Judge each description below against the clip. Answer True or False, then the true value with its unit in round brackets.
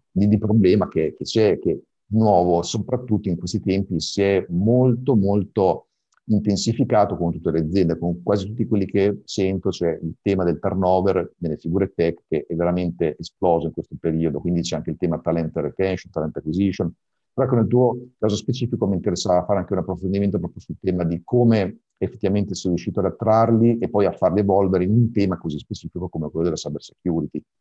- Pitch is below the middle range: True (95 Hz)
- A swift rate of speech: True (190 wpm)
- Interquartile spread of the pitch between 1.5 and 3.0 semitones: False (3.6 semitones)